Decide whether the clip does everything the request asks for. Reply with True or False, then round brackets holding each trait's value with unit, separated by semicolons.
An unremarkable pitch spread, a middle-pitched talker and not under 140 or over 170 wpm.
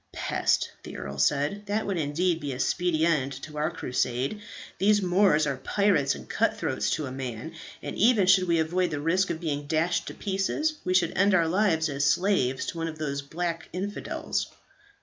False (4.7 semitones; 165 Hz; 195 wpm)